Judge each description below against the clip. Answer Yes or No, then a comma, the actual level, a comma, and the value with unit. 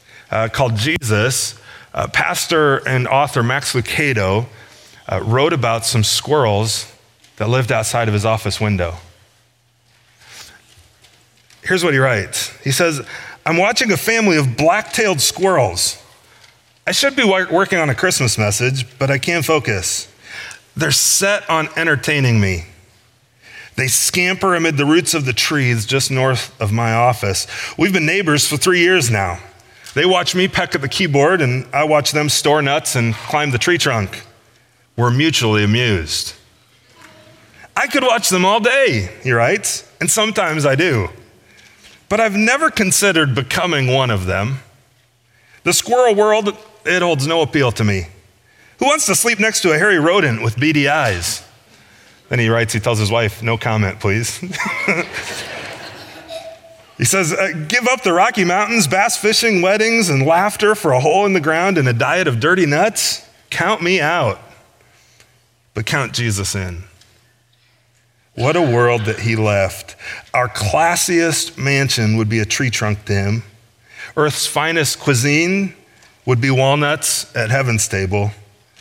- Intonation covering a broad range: Yes, wide, 6.5 semitones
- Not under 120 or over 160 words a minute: Yes, average, 150 wpm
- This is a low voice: Yes, low, 125 Hz